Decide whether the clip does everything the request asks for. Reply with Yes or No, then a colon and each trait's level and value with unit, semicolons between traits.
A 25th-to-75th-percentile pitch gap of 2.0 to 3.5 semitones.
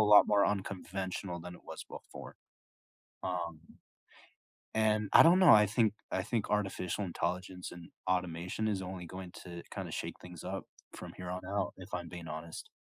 Yes: narrow, 2.6 semitones